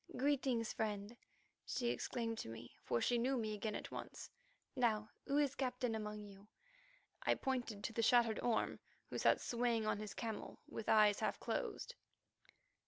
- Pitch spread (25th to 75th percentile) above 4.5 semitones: No, narrow, 2.6 semitones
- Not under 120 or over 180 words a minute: Yes, average, 165 wpm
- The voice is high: Yes, high, 225 Hz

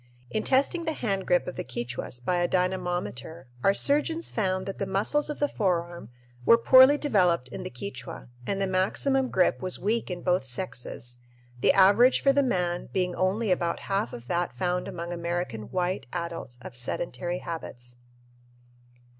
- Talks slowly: No, average, 170 wpm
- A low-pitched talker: No, medium, 180 Hz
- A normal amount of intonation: Yes, average, 3.6 semitones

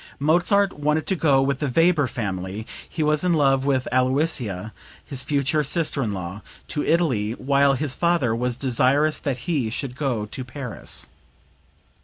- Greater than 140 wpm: Yes, average, 160 wpm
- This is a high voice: No, low, 135 Hz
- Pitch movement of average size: Yes, average, 3.8 semitones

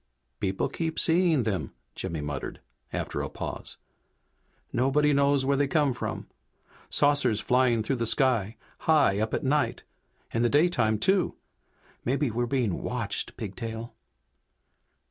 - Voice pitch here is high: No, low, 125 Hz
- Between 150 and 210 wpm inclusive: No, slow, 135 wpm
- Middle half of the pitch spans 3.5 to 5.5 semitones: Yes, average, 4.6 semitones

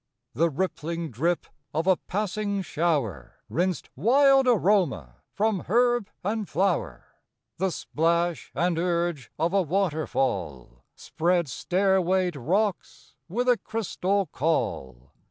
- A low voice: No, medium, 175 Hz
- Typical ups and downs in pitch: Yes, average, 4.3 semitones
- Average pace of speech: No, slow, 110 wpm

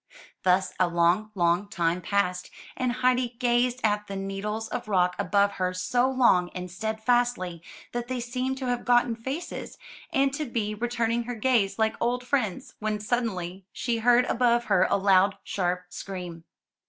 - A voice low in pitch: No, high, 215 Hz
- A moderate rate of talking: Yes, average, 165 wpm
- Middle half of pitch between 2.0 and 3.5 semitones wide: No, average, 4.7 semitones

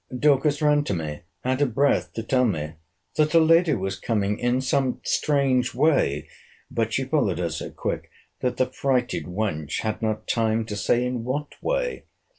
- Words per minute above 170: Yes, average, 180 wpm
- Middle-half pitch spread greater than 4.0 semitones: Yes, average, 5.1 semitones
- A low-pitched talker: Yes, low, 125 Hz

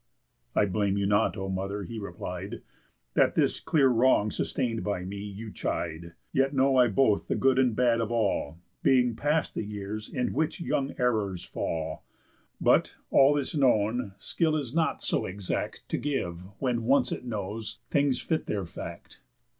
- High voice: No, low, 115 Hz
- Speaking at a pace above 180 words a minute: No, average, 170 wpm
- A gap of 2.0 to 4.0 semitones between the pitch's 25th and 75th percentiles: No, average, 5.0 semitones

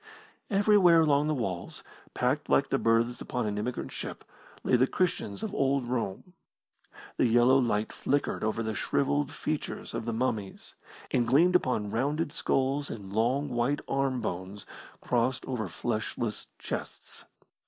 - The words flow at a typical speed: Yes, average, 145 wpm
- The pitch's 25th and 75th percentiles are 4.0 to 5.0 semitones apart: Yes, average, 4.3 semitones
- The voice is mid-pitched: No, low, 125 Hz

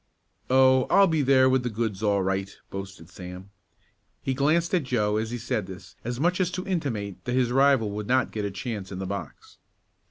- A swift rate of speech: Yes, fast, 210 wpm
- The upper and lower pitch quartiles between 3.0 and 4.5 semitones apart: No, average, 4.9 semitones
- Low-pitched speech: Yes, low, 120 Hz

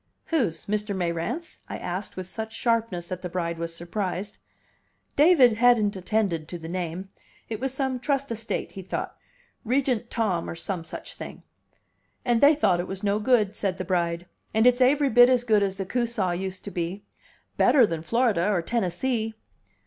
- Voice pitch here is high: Yes, high, 205 Hz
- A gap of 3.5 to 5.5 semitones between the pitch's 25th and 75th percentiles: Yes, average, 5.2 semitones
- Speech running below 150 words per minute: No, average, 180 wpm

